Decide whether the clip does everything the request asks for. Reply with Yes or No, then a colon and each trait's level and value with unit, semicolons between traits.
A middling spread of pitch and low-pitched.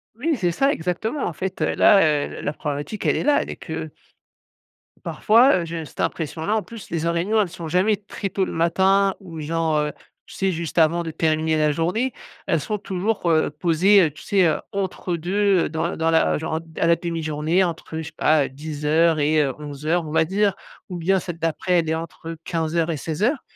No: average, 3.3 semitones; medium, 165 Hz